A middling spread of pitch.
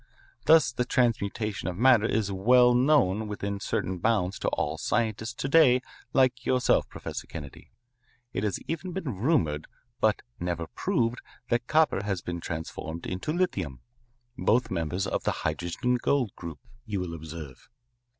No: wide, 5.9 semitones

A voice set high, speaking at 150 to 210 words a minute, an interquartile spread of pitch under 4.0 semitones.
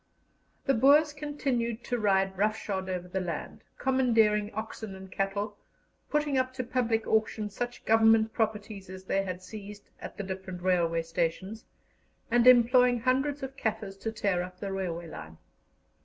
No: high, 215 Hz; average, 155 wpm; average, 4.3 semitones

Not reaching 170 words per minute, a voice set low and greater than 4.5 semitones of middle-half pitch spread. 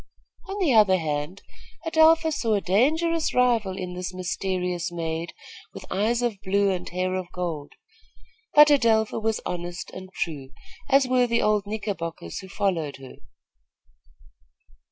No: average, 140 wpm; high, 195 Hz; average, 5.1 semitones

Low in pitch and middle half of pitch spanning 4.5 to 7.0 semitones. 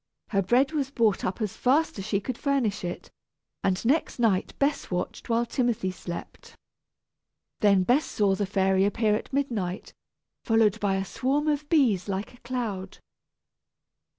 No: high, 215 Hz; average, 5.0 semitones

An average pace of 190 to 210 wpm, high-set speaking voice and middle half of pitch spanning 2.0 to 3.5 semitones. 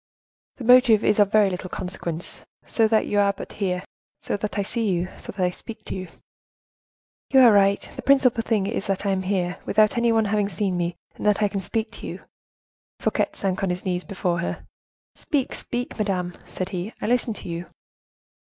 Yes: average, 200 wpm; high, 200 Hz; average, 3.1 semitones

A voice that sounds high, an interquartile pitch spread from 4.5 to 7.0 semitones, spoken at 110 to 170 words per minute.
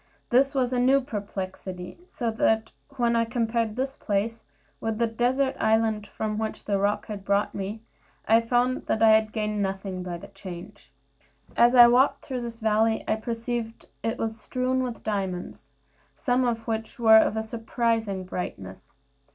No: high, 225 Hz; narrow, 2.6 semitones; average, 165 wpm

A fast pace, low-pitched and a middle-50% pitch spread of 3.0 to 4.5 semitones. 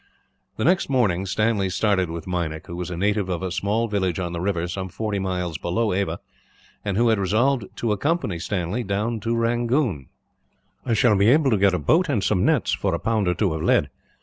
Yes: fast, 215 wpm; low, 100 Hz; average, 4.2 semitones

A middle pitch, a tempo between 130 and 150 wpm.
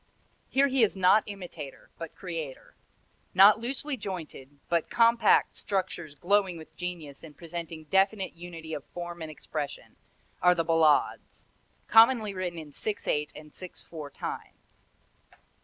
Yes: medium, 175 Hz; average, 140 wpm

